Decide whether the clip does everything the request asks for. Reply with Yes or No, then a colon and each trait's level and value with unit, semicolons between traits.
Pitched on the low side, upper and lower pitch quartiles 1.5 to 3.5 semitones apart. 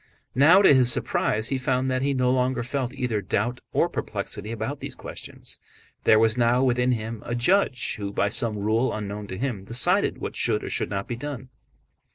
Yes: low, 120 Hz; average, 3.1 semitones